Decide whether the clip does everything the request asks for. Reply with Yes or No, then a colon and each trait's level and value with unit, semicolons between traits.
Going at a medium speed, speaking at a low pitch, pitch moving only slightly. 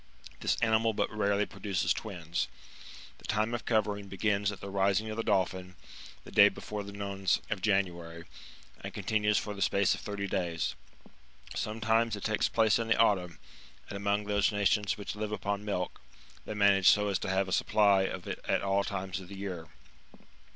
Yes: average, 190 wpm; low, 100 Hz; narrow, 1.7 semitones